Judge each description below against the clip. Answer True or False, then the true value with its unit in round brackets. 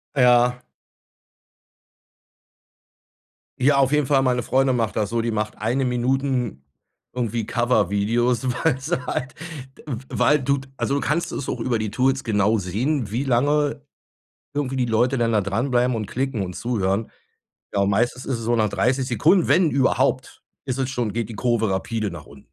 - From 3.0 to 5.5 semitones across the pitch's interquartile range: True (3.3 semitones)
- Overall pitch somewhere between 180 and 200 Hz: False (125 Hz)